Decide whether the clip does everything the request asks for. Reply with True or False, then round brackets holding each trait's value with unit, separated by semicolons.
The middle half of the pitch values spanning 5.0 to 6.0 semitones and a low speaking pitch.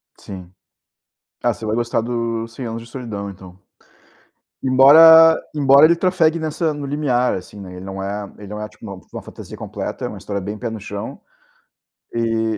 True (5.4 semitones; 115 Hz)